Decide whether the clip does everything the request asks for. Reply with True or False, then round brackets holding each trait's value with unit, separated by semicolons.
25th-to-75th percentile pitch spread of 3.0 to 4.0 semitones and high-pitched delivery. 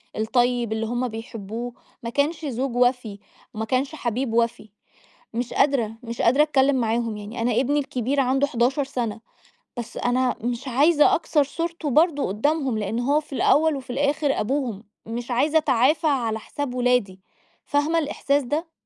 True (3.7 semitones; 250 Hz)